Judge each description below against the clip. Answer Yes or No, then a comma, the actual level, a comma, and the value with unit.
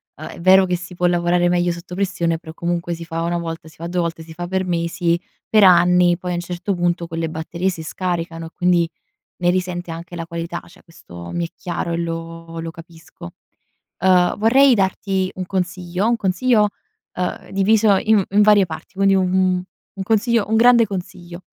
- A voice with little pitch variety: Yes, narrow, 2.0 semitones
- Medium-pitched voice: Yes, medium, 175 Hz